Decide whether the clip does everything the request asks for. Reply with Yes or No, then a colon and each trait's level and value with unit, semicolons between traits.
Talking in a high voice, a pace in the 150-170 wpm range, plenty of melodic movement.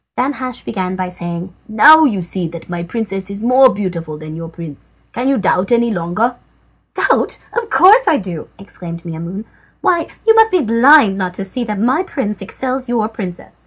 No: high, 205 Hz; average, 190 wpm; wide, 6.3 semitones